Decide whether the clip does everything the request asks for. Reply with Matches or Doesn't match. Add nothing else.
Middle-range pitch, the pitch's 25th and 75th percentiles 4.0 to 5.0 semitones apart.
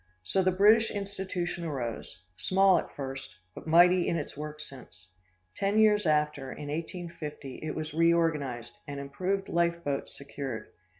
Matches